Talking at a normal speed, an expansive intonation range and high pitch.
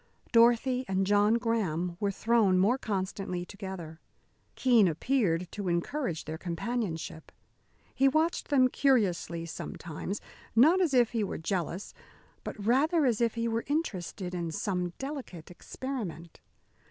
No: slow, 130 wpm; wide, 5.9 semitones; high, 205 Hz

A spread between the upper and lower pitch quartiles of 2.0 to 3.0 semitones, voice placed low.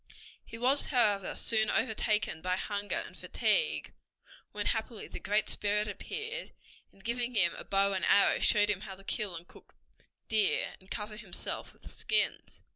No: narrow, 2.6 semitones; high, 210 Hz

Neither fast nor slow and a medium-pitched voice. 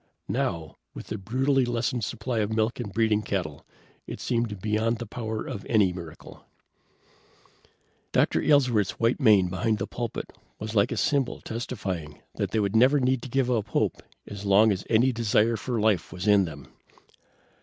No: average, 165 wpm; low, 110 Hz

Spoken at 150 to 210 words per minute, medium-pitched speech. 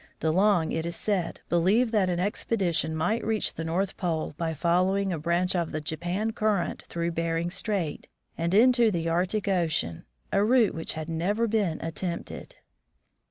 Yes: average, 165 wpm; medium, 175 Hz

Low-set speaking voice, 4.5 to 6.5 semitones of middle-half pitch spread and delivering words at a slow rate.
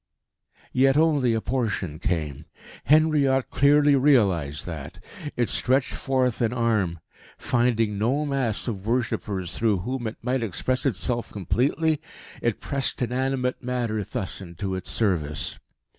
Yes: low, 120 Hz; average, 5.2 semitones; slow, 130 wpm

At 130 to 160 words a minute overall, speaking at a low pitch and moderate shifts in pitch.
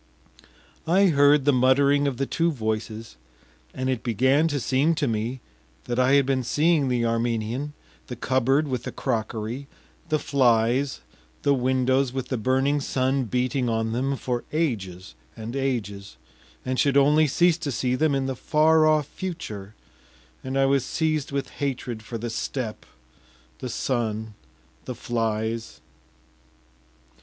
Yes: average, 150 wpm; low, 130 Hz; average, 3.4 semitones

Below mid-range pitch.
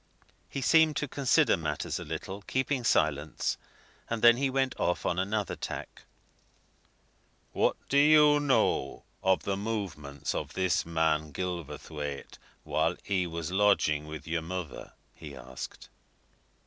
Yes: very low, 90 Hz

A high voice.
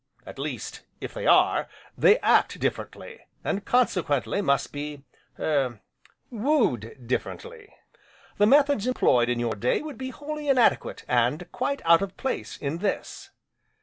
Yes: high, 200 Hz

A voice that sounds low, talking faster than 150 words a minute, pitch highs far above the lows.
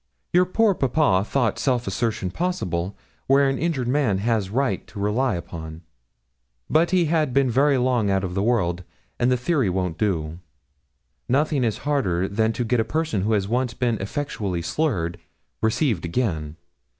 Yes: low, 115 Hz; average, 165 wpm; wide, 6.4 semitones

